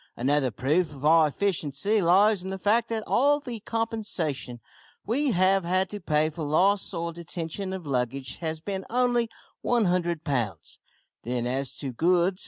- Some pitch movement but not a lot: No, wide, 5.7 semitones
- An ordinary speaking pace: Yes, average, 160 wpm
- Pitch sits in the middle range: Yes, medium, 175 Hz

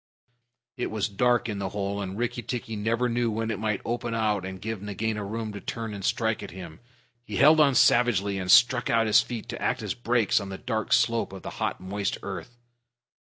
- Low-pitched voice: Yes, low, 110 Hz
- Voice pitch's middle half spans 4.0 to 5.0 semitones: No, average, 2.9 semitones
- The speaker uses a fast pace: Yes, fast, 220 wpm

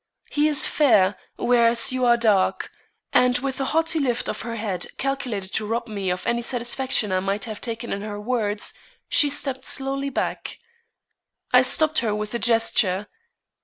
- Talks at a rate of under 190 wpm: Yes, average, 170 wpm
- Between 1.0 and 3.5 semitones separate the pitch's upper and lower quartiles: No, average, 4.1 semitones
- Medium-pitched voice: No, high, 235 Hz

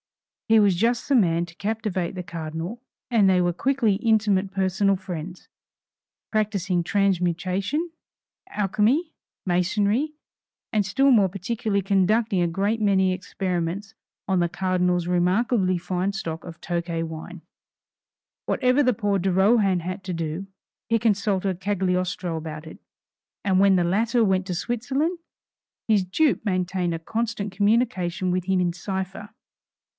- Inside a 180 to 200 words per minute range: No, slow, 135 wpm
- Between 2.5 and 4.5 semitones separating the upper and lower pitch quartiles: Yes, average, 3.2 semitones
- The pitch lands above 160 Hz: Yes, high, 190 Hz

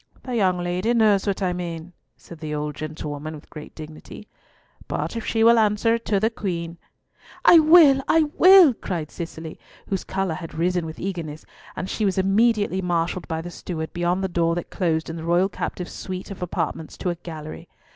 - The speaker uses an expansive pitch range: No, average, 3.9 semitones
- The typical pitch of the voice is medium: Yes, medium, 180 Hz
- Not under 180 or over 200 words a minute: Yes, average, 195 wpm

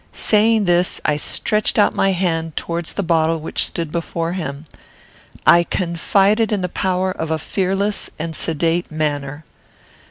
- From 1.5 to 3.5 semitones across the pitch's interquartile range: Yes, average, 3.2 semitones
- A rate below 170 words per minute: Yes, average, 150 wpm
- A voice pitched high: No, medium, 170 Hz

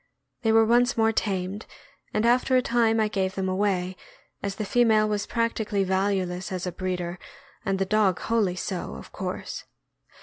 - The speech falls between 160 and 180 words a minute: Yes, average, 170 wpm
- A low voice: No, high, 200 Hz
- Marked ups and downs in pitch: No, average, 3.0 semitones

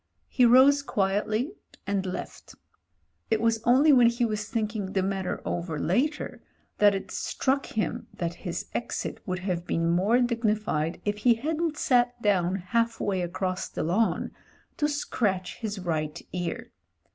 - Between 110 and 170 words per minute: Yes, average, 145 wpm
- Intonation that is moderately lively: Yes, average, 4.7 semitones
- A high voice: Yes, high, 210 Hz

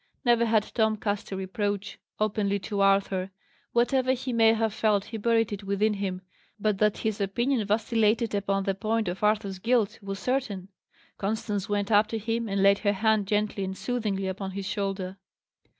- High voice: Yes, high, 210 Hz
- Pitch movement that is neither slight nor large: No, narrow, 2.1 semitones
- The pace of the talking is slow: No, average, 180 wpm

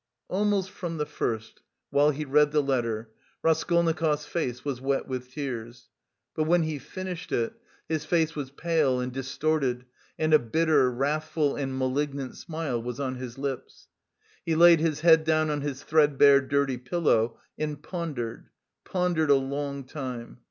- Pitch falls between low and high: Yes, medium, 145 Hz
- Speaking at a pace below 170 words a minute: Yes, average, 155 wpm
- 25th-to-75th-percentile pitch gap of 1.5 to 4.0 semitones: Yes, average, 3.4 semitones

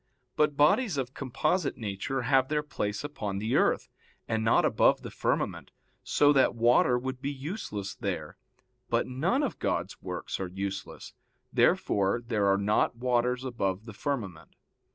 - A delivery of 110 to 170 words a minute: Yes, average, 155 wpm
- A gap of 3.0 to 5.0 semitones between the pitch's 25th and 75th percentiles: No, wide, 5.5 semitones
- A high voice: No, low, 125 Hz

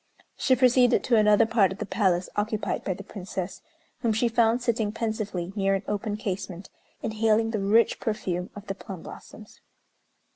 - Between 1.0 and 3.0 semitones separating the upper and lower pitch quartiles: Yes, narrow, 2.5 semitones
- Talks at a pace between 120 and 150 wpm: No, average, 170 wpm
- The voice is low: No, high, 210 Hz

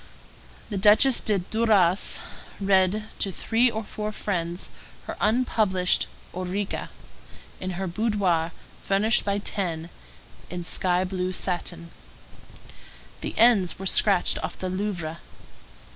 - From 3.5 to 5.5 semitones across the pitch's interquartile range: No, average, 2.8 semitones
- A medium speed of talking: No, slow, 115 wpm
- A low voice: No, high, 190 Hz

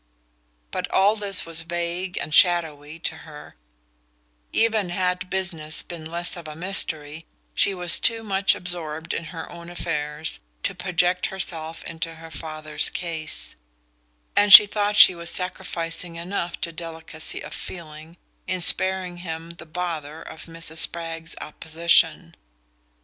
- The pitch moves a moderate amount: No, narrow, 2.1 semitones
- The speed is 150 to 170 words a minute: No, average, 140 wpm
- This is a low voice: No, medium, 170 Hz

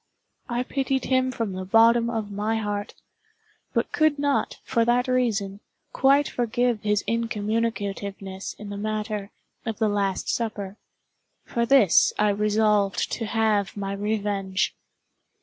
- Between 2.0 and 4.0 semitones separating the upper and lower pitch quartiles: Yes, narrow, 2.6 semitones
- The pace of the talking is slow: Yes, slow, 130 wpm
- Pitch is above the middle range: Yes, high, 215 Hz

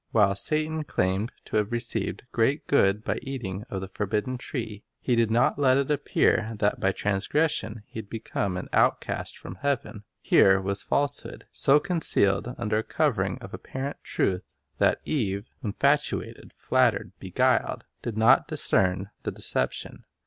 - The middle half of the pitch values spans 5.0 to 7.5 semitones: Yes, average, 5.3 semitones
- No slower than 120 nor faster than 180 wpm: Yes, average, 150 wpm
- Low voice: Yes, low, 110 Hz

